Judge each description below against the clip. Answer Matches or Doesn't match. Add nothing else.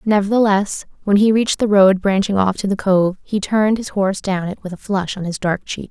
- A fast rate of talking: Matches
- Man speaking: Doesn't match